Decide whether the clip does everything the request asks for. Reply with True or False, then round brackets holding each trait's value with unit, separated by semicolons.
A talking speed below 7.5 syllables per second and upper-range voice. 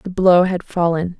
False (4.4 syllables/s; 175 Hz)